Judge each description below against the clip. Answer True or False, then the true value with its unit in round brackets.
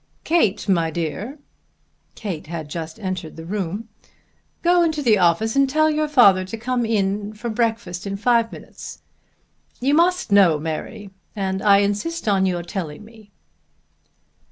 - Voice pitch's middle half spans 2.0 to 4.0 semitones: False (4.5 semitones)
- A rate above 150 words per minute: False (145 wpm)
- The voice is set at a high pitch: True (205 Hz)